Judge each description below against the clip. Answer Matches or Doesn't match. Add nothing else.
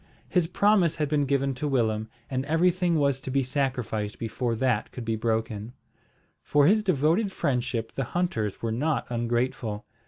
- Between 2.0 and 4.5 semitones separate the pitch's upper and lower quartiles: Doesn't match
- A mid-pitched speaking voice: Doesn't match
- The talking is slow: Doesn't match